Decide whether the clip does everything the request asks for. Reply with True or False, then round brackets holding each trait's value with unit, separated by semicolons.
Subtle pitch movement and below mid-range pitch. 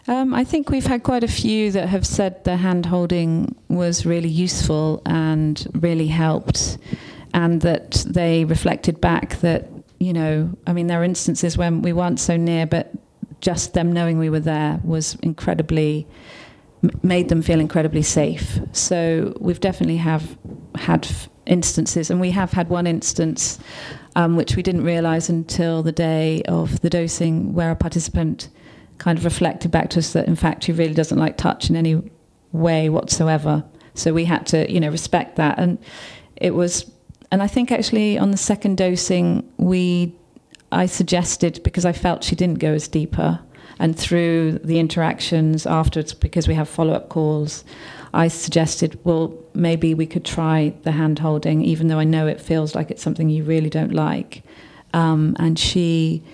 False (1.8 semitones; 165 Hz)